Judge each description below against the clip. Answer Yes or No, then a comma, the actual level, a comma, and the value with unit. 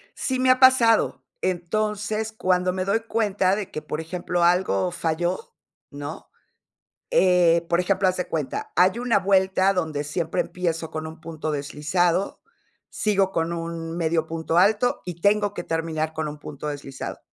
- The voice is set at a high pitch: No, medium, 175 Hz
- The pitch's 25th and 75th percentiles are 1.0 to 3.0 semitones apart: No, average, 3.5 semitones